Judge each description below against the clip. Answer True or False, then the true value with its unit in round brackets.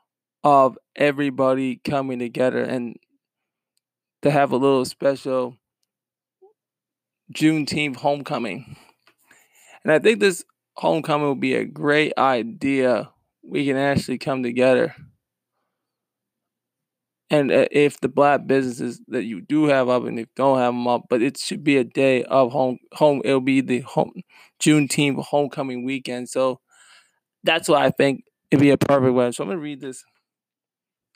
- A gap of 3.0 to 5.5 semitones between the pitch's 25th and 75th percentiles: False (2.4 semitones)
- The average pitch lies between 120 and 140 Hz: True (135 Hz)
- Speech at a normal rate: True (145 wpm)